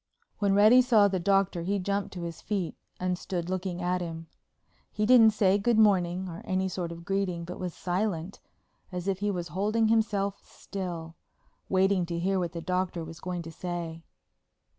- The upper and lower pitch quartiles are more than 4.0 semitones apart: No, narrow, 2.5 semitones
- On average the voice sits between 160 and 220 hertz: Yes, medium, 185 Hz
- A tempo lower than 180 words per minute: No, average, 185 wpm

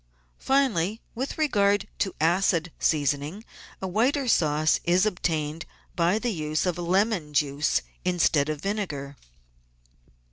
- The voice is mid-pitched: Yes, medium, 175 Hz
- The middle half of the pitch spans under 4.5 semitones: No, average, 5.2 semitones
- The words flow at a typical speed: No, slow, 115 wpm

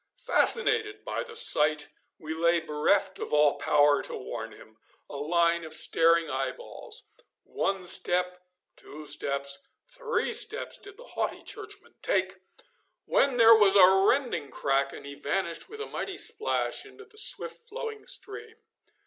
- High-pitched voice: No, medium, 180 Hz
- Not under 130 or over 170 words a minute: Yes, average, 150 wpm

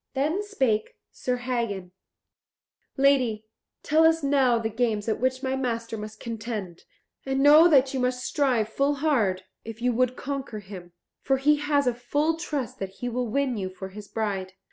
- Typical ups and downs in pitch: Yes, average, 4.3 semitones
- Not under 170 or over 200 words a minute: Yes, average, 175 wpm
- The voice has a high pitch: Yes, very high, 250 Hz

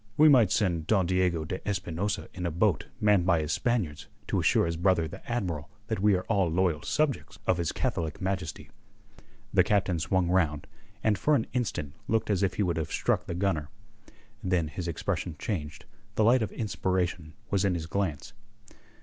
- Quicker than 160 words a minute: Yes, average, 185 wpm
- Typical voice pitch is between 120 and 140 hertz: No, very low, 90 Hz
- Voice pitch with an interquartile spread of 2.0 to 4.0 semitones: Yes, average, 3.7 semitones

